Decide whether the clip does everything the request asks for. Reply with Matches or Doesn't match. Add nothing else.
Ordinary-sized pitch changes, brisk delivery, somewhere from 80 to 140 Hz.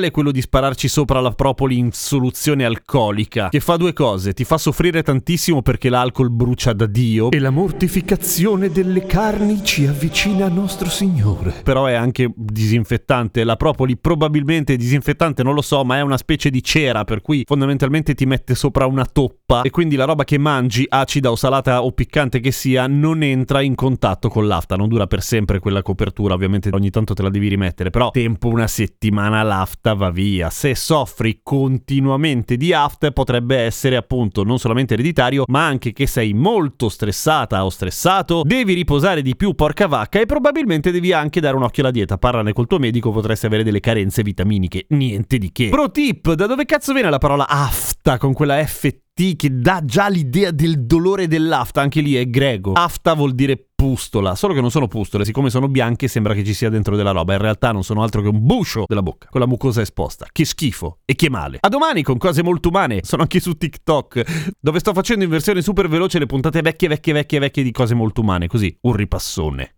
Doesn't match